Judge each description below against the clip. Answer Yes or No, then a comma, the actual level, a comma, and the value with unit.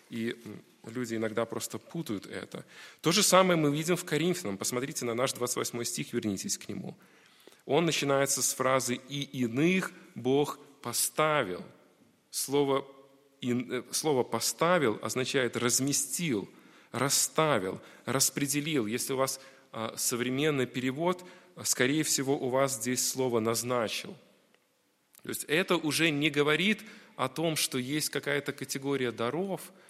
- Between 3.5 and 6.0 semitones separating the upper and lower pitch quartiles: Yes, average, 3.8 semitones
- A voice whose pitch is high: No, low, 135 Hz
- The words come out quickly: No, average, 120 wpm